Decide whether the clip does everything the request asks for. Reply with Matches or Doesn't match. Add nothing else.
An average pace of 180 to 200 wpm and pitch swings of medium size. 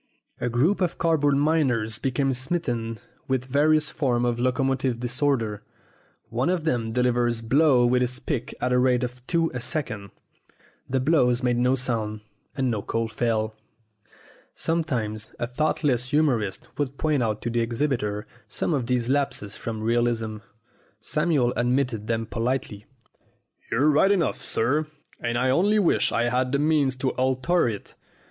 Doesn't match